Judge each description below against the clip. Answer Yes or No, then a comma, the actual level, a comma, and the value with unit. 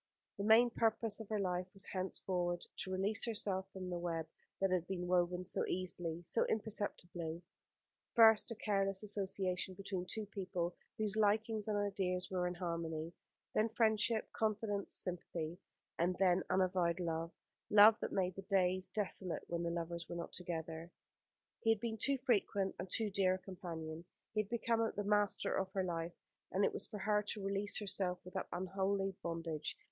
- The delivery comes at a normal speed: Yes, average, 170 wpm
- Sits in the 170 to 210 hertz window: Yes, high, 190 Hz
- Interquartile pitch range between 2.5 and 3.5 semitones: Yes, average, 2.8 semitones